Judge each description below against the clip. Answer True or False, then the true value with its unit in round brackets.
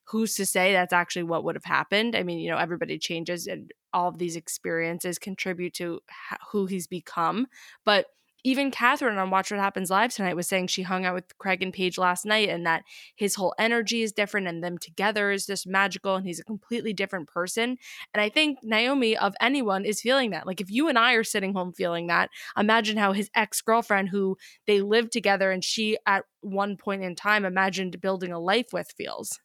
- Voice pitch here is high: True (195 Hz)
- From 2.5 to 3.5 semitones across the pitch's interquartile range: True (3.1 semitones)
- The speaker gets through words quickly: True (215 wpm)